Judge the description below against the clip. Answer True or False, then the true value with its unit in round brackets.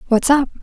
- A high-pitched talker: True (260 Hz)